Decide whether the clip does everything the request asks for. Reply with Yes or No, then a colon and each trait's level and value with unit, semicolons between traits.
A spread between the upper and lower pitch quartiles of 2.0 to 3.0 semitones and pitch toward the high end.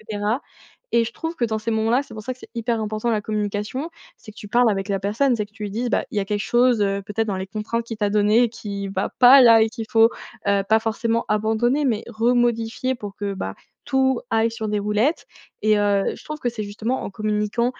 Yes: narrow, 2.4 semitones; high, 220 Hz